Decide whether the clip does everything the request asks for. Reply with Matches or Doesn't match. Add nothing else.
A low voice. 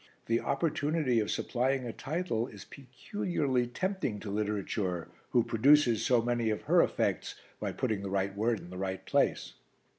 Matches